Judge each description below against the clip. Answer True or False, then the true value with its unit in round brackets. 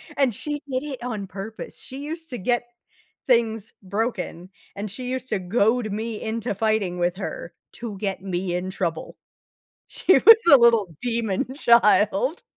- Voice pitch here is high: True (220 Hz)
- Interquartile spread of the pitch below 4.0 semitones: False (4.3 semitones)